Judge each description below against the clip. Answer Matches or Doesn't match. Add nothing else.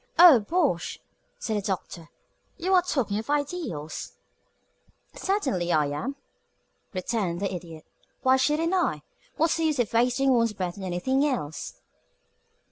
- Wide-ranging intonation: Matches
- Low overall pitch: Doesn't match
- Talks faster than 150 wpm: Doesn't match